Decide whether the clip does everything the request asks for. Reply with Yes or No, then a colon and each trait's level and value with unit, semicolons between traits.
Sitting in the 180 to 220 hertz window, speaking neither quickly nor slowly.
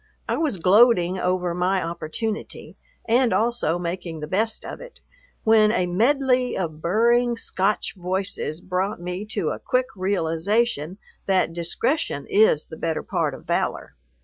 Yes: high, 190 Hz; average, 145 wpm